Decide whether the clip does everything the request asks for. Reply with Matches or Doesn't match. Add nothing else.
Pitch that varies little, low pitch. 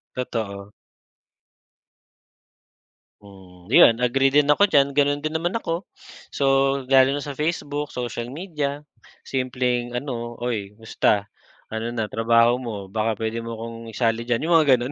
Doesn't match